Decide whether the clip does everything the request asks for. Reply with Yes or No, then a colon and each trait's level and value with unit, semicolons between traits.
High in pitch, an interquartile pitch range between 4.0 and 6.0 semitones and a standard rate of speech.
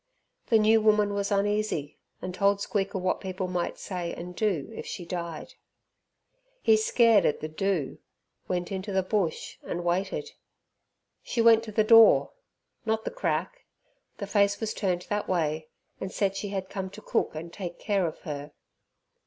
No: high, 195 Hz; average, 3.2 semitones; average, 170 wpm